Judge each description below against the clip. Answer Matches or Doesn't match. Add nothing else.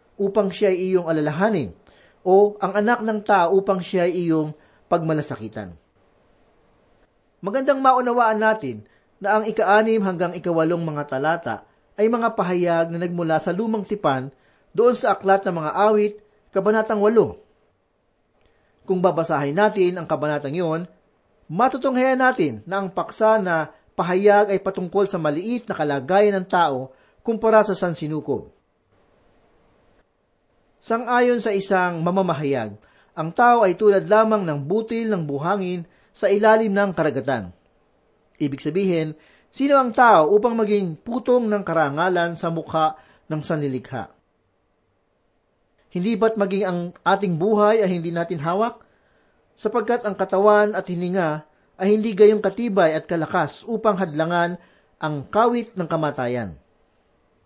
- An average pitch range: Matches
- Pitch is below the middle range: Doesn't match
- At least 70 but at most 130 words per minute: Matches